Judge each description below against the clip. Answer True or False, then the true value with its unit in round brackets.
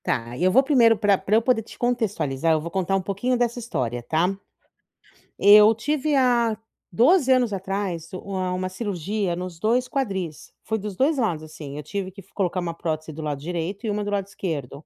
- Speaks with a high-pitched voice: True (195 Hz)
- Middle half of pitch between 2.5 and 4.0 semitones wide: False (5.3 semitones)